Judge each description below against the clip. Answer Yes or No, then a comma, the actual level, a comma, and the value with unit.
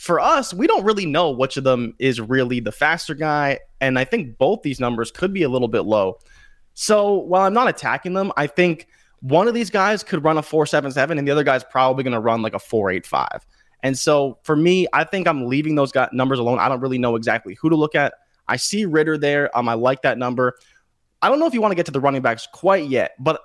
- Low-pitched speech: No, medium, 145 Hz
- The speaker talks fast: Yes, fast, 250 wpm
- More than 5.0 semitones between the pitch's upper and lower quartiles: Yes, wide, 5.4 semitones